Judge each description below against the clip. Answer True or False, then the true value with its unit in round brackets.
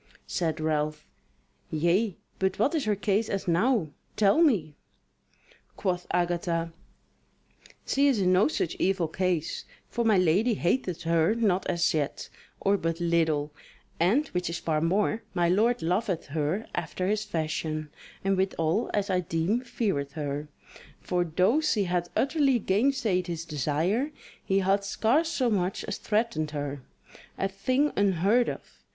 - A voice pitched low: False (185 Hz)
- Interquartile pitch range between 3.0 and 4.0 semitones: False (4.6 semitones)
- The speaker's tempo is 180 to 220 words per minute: False (145 wpm)